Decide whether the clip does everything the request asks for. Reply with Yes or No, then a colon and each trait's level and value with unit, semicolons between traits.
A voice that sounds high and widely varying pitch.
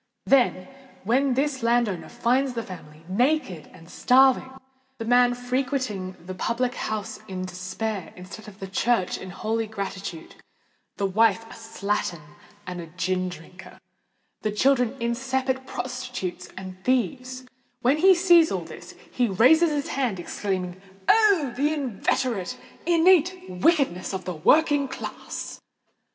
Yes: high, 235 Hz; wide, 5.8 semitones